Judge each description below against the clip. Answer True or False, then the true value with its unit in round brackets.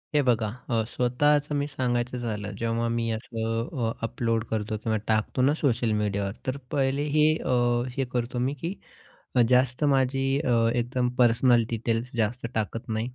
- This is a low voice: True (120 Hz)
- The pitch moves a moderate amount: False (2.3 semitones)